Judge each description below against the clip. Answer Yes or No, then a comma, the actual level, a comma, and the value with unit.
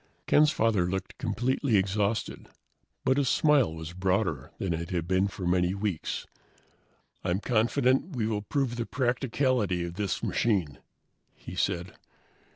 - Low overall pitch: Yes, low, 100 Hz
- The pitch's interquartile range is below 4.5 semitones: No, average, 5.3 semitones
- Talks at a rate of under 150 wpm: Yes, average, 140 wpm